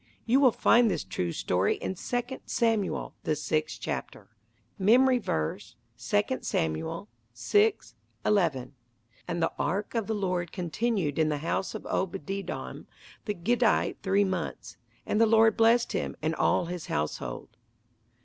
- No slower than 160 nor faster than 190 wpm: No, average, 140 wpm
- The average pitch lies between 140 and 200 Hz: Yes, high, 190 Hz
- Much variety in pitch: Yes, wide, 6.5 semitones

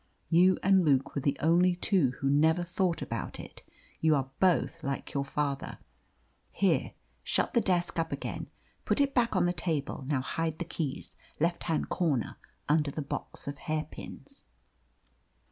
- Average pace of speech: Yes, average, 160 wpm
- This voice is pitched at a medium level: Yes, medium, 160 Hz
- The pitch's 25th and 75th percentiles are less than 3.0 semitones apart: No, average, 3.7 semitones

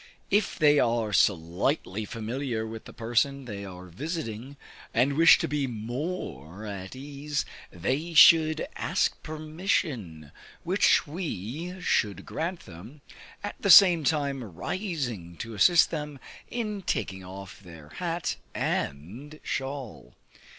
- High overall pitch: No, low, 130 Hz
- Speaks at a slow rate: Yes, slow, 120 wpm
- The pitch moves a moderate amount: No, wide, 7.8 semitones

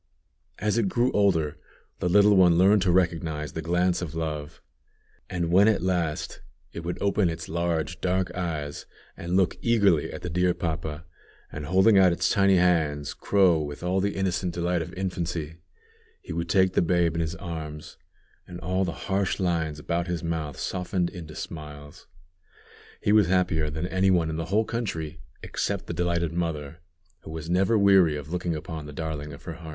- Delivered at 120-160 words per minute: No, average, 185 wpm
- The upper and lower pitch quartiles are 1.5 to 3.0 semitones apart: Yes, average, 2.7 semitones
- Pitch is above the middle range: No, very low, 85 Hz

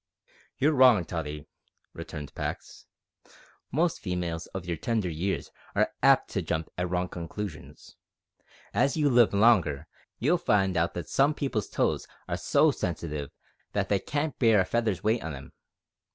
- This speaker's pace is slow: No, average, 150 wpm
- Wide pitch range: Yes, wide, 6.3 semitones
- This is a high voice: No, very low, 95 Hz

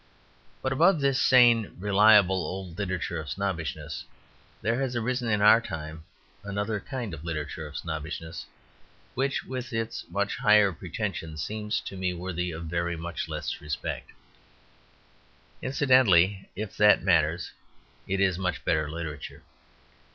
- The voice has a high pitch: No, very low, 95 Hz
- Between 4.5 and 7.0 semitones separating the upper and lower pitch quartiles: Yes, average, 4.9 semitones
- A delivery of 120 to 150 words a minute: Yes, slow, 135 wpm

